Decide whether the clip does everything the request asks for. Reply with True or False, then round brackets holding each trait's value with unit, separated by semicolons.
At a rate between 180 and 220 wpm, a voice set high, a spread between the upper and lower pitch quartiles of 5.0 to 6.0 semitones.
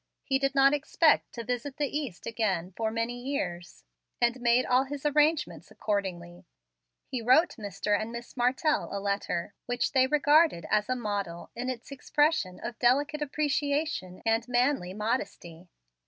False (155 wpm; 245 Hz; 5.6 semitones)